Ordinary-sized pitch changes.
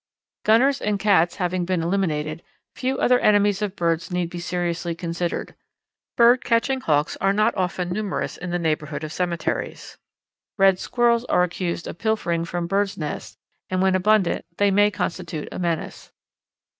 Yes: average, 3.3 semitones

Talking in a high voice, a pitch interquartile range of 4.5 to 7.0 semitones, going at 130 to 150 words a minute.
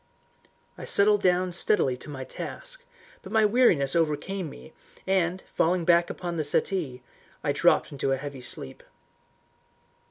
No: medium, 170 Hz; wide, 5.4 semitones; average, 140 wpm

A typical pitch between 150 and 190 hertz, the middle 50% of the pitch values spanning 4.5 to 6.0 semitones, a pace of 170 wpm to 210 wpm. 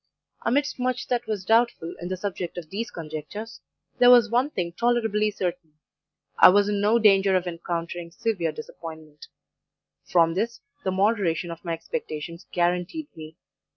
No: medium, 185 Hz; average, 5.1 semitones; average, 155 wpm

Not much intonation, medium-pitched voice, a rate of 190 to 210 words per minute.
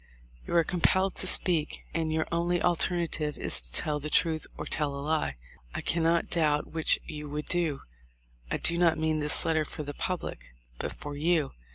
Yes: narrow, 2.2 semitones; medium, 160 Hz; average, 195 wpm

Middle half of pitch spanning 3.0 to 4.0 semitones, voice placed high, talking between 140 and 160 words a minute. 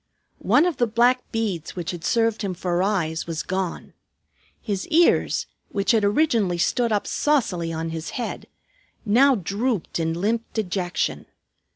No: average, 5.0 semitones; high, 205 Hz; average, 150 wpm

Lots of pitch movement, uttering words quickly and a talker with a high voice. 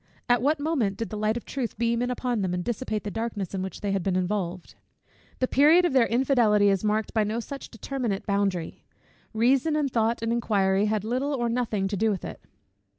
No: average, 3.7 semitones; fast, 215 wpm; high, 225 Hz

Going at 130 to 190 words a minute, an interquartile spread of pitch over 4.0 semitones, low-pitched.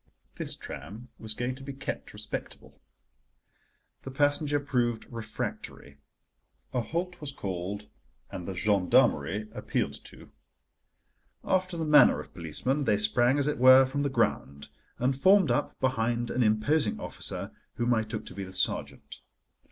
Yes: average, 145 wpm; average, 5.0 semitones; low, 120 Hz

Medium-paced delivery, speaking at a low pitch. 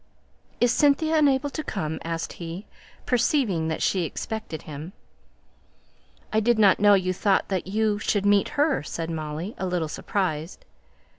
No: average, 150 wpm; high, 195 Hz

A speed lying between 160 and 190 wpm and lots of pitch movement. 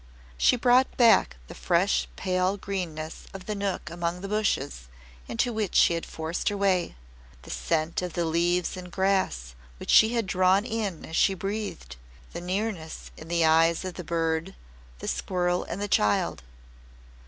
No: average, 165 wpm; average, 3.5 semitones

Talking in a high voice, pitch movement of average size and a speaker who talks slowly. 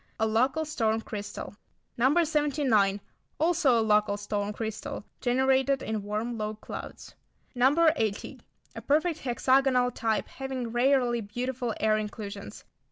Yes: high, 240 Hz; average, 3.8 semitones; slow, 125 wpm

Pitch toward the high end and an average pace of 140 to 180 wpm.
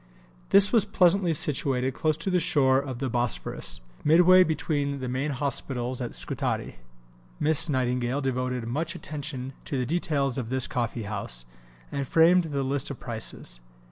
No: low, 135 Hz; average, 155 wpm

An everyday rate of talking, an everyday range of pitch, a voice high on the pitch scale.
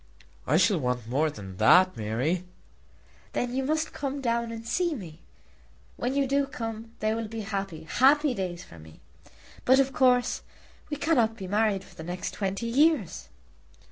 No: average, 170 wpm; wide, 7.2 semitones; high, 225 Hz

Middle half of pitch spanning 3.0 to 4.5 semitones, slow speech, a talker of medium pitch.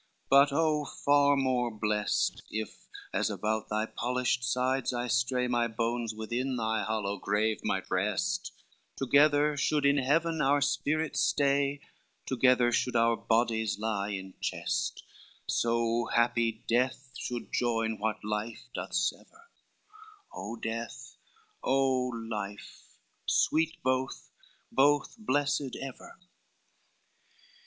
No: average, 4.0 semitones; slow, 115 wpm; low, 125 Hz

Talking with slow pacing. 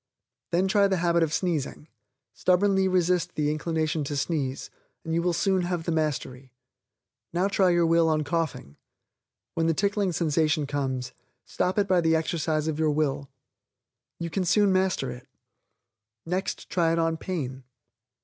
No: average, 160 wpm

